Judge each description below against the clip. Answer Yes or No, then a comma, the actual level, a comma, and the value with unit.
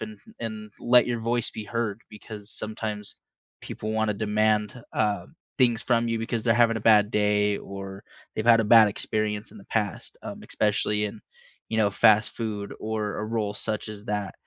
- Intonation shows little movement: Yes, narrow, 1.5 semitones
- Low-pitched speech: Yes, low, 110 Hz